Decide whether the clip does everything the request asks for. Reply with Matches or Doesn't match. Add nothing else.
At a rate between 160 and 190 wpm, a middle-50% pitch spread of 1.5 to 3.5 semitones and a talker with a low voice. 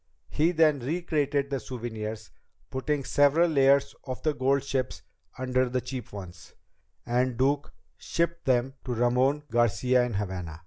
Doesn't match